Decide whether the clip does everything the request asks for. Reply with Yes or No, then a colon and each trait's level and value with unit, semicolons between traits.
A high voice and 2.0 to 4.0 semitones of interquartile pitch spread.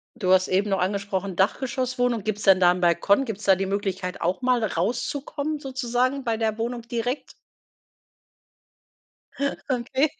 No: high, 220 Hz; average, 4.6 semitones